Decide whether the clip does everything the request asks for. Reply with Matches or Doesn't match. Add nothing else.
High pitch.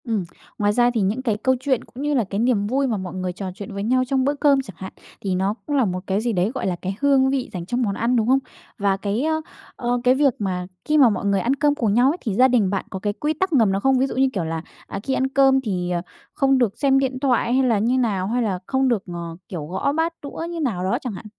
Matches